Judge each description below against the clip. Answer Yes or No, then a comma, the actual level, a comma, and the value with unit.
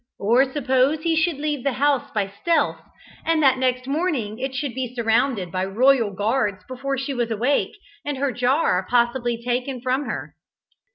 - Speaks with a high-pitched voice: Yes, very high, 255 Hz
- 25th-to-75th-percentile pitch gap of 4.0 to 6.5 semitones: No, average, 3.0 semitones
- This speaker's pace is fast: No, average, 170 wpm